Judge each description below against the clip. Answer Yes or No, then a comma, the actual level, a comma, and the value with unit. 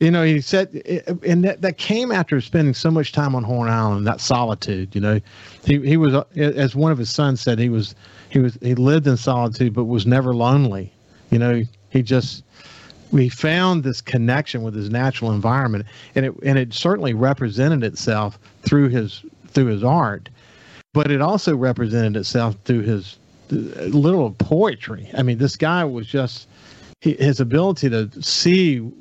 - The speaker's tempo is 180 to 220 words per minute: No, average, 170 wpm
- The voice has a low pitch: Yes, low, 130 Hz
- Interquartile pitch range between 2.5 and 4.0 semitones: No, average, 4.4 semitones